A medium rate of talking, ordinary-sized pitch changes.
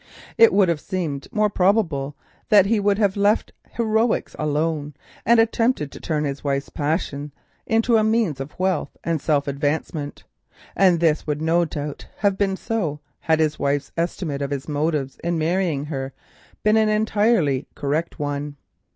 No: average, 160 wpm; wide, 5.8 semitones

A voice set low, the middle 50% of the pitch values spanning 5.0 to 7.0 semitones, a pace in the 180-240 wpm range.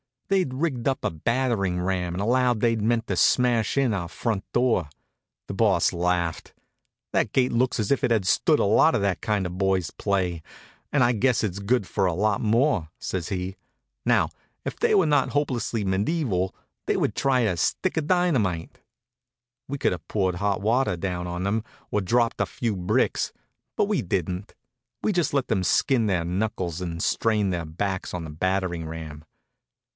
Yes: low, 100 Hz; wide, 5.4 semitones; average, 185 wpm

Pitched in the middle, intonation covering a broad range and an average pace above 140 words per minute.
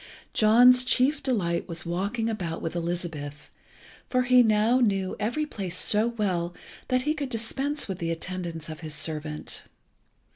No: high, 200 Hz; wide, 6.5 semitones; average, 150 wpm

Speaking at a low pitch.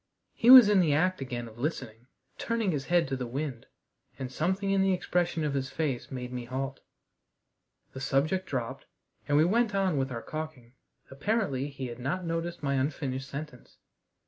No: medium, 145 Hz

